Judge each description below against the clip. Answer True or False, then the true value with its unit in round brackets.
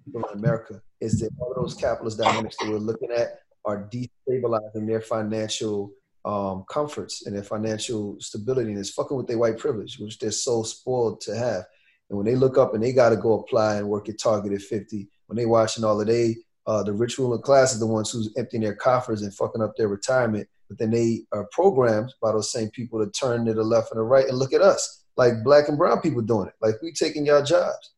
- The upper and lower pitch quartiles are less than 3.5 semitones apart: True (2.8 semitones)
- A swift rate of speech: True (230 wpm)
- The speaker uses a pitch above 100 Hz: True (110 Hz)